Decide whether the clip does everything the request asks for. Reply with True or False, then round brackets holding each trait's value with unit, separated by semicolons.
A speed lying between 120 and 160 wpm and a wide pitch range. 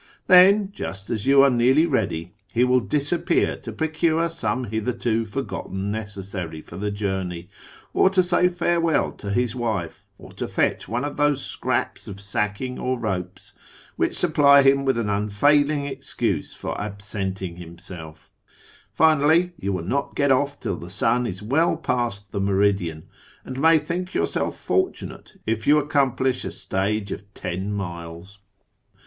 True (155 wpm; 6.6 semitones)